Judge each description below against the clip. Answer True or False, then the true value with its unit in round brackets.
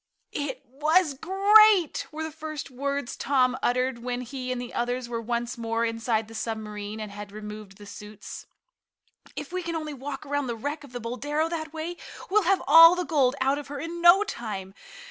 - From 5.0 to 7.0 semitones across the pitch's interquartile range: True (5.3 semitones)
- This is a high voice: True (265 Hz)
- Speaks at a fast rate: False (195 wpm)